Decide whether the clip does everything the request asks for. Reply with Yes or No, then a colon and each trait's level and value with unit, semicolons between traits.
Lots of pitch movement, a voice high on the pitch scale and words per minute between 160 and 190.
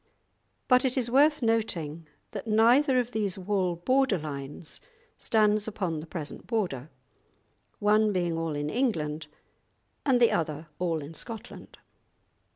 No: wide, 6.3 semitones; high, 205 Hz; slow, 135 wpm